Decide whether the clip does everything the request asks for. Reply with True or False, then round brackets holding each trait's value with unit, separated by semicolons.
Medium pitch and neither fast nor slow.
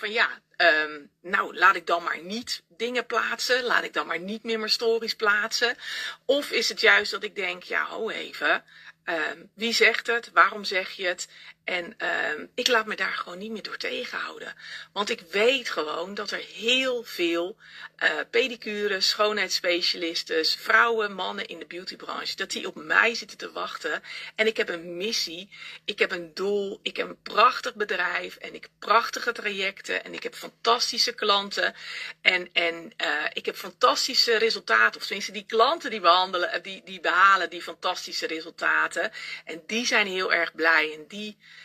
False (210 Hz; 175 wpm)